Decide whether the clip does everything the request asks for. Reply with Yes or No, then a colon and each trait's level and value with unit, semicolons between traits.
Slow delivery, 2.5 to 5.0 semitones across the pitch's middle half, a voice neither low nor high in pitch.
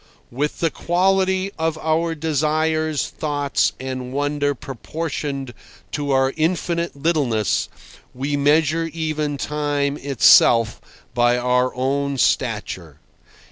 Yes: slow, 100 wpm; average, 3.0 semitones; medium, 145 Hz